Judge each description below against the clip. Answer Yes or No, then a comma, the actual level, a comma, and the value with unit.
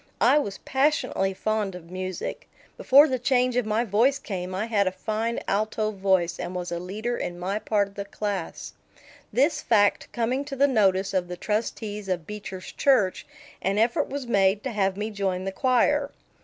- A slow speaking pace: No, average, 185 wpm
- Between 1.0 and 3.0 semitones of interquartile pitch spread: No, average, 4.0 semitones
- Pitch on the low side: No, high, 210 Hz